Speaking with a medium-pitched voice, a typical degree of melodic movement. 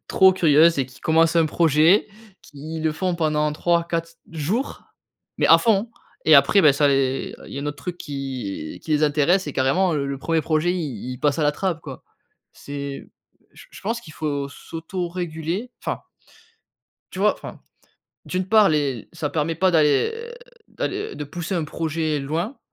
Yes: medium, 160 Hz; average, 3.4 semitones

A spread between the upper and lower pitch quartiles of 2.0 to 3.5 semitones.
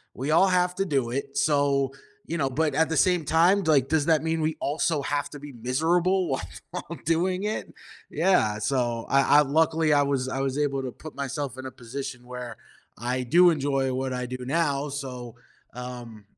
No: average, 4.0 semitones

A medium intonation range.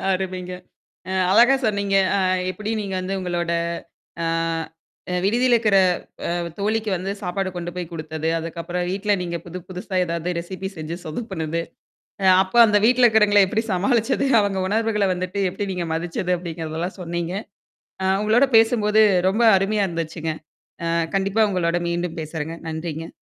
Yes: average, 3.6 semitones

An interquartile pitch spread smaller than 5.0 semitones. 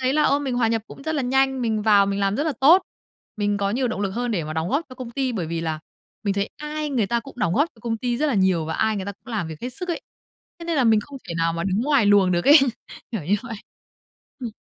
No: average, 5.3 semitones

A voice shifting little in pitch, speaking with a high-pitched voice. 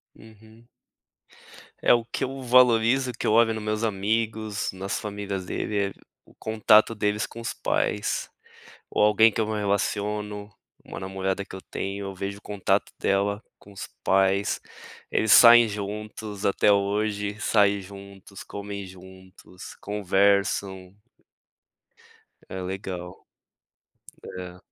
No: narrow, 1.9 semitones; low, 100 Hz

